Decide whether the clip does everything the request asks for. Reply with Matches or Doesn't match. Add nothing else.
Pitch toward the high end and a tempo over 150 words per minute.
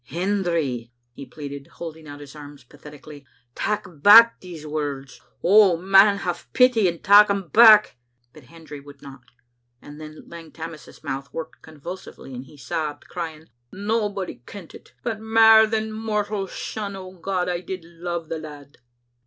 Doesn't match